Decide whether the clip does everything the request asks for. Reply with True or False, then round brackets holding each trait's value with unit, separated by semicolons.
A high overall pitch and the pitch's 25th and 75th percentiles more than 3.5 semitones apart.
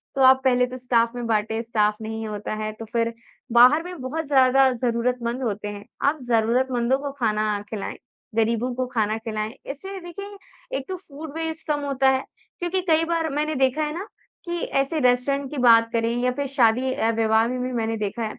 True (250 Hz; 3.9 semitones)